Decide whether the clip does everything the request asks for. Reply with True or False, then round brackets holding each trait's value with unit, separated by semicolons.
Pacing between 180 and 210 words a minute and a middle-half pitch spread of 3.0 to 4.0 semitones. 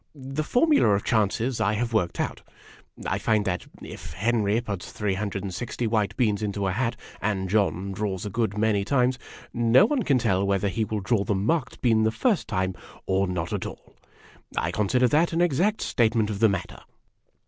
True (190 wpm; 3.7 semitones)